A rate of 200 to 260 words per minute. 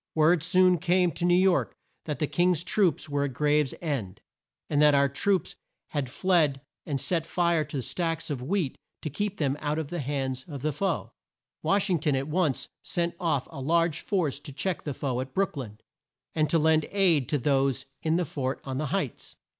Yes: fast, 205 wpm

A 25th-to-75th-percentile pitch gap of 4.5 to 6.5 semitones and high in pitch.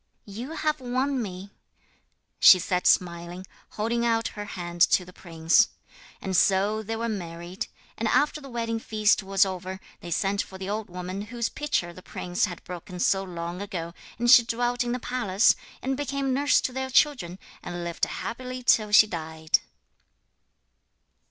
Yes: average, 5.0 semitones; high, 200 Hz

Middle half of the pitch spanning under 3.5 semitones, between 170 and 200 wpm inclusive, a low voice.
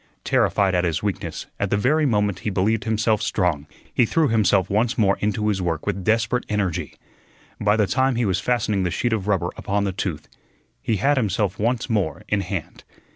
Yes: average, 3.0 semitones; average, 195 wpm; low, 105 Hz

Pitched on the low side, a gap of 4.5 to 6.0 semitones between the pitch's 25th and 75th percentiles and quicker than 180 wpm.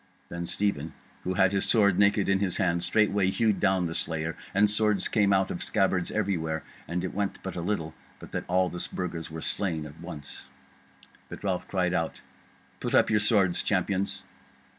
No: very low, 95 Hz; average, 2.7 semitones; average, 190 wpm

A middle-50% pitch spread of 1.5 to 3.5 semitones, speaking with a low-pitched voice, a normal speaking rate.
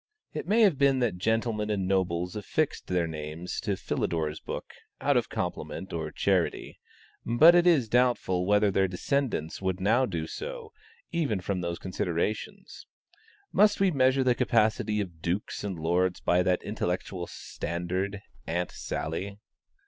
No: wide, 5.6 semitones; very low, 95 Hz; average, 150 wpm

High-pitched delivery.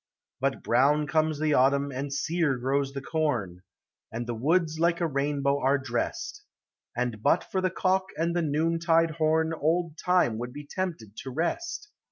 No: medium, 150 Hz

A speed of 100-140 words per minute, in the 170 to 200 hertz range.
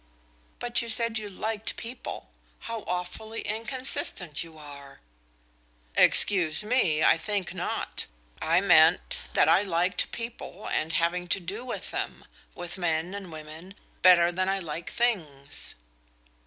Yes: slow, 135 wpm; medium, 185 Hz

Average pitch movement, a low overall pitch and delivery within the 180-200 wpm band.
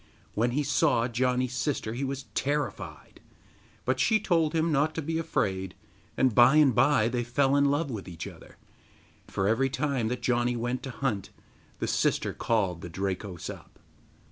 No: average, 4.3 semitones; low, 125 Hz; average, 170 wpm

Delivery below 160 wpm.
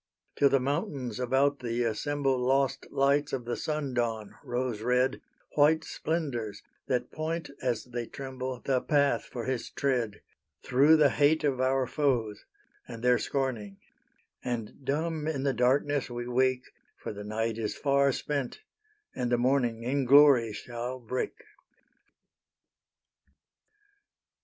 Yes: slow, 135 wpm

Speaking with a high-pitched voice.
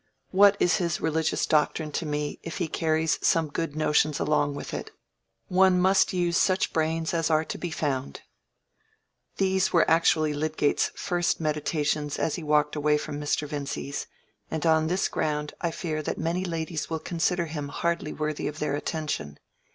No: medium, 160 Hz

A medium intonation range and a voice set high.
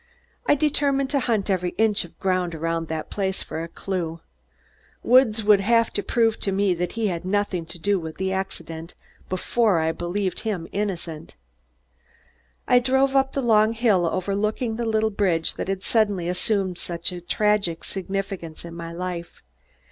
Yes: average, 4.1 semitones; high, 195 Hz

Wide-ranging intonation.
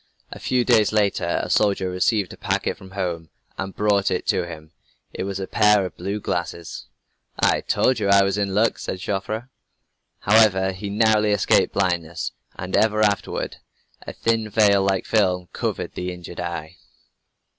No: narrow, 2.6 semitones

